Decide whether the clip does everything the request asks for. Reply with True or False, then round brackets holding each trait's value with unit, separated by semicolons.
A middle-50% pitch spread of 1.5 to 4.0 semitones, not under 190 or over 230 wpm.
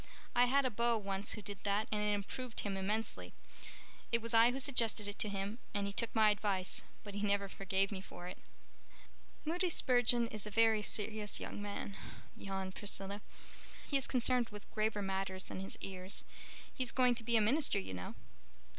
True (3.0 semitones; 195 wpm)